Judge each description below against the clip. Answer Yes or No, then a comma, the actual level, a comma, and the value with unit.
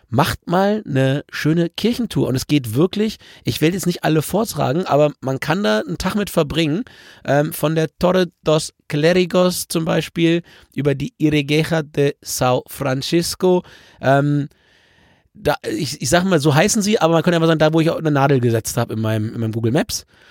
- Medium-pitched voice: Yes, medium, 155 Hz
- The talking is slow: No, fast, 190 wpm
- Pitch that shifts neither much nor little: Yes, average, 4.0 semitones